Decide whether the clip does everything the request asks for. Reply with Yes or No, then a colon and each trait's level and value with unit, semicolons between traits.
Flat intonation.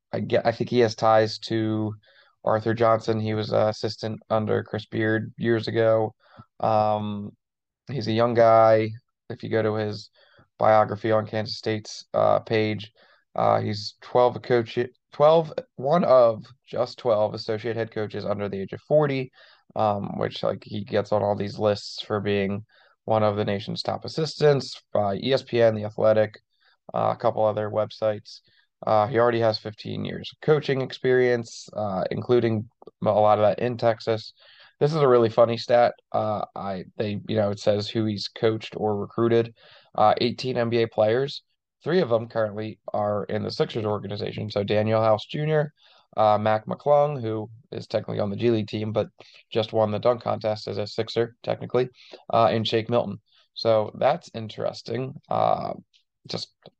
Yes: narrow, 1.9 semitones